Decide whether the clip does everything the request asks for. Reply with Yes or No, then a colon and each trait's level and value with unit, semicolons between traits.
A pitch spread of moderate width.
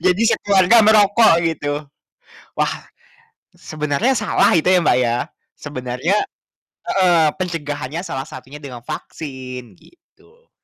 No: wide, 6.3 semitones